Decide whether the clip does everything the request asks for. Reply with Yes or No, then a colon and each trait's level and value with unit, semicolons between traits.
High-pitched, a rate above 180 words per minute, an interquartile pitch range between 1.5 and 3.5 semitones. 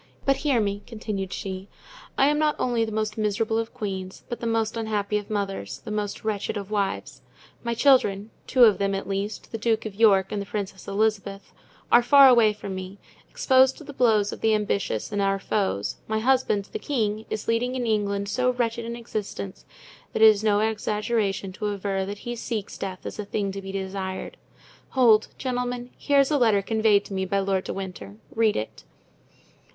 Yes: high, 210 Hz; average, 200 wpm; average, 2.7 semitones